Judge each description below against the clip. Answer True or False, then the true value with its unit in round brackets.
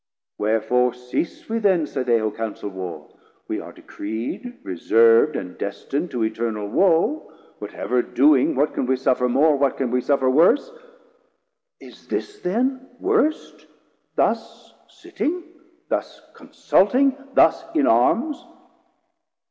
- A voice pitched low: True (130 Hz)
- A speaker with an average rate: False (130 wpm)